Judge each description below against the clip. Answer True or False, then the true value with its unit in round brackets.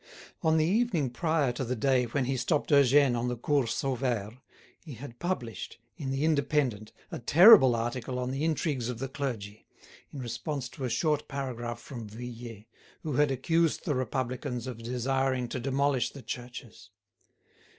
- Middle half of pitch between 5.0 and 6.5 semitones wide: False (3.2 semitones)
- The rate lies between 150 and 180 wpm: True (165 wpm)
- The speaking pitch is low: True (130 Hz)